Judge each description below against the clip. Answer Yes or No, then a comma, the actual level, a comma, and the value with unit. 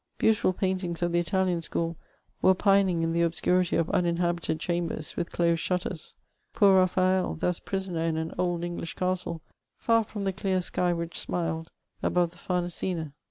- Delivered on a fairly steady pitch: Yes, narrow, 1.7 semitones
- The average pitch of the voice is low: No, medium, 175 Hz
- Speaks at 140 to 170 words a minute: Yes, average, 160 wpm